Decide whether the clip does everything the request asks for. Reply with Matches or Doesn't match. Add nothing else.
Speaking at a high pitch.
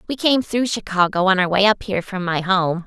Matches